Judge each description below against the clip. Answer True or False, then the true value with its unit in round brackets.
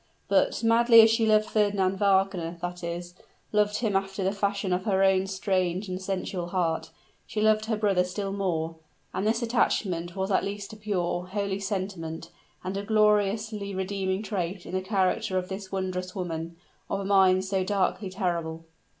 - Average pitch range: False (2.0 semitones)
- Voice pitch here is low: False (195 Hz)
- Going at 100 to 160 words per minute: False (175 wpm)